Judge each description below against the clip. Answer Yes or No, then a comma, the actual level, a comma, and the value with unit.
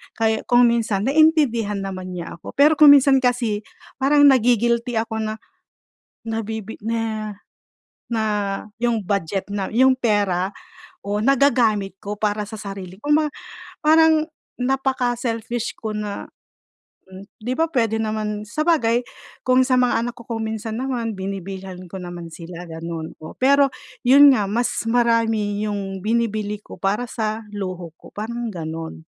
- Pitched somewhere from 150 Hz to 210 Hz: No, high, 220 Hz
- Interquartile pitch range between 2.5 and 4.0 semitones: Yes, average, 3.5 semitones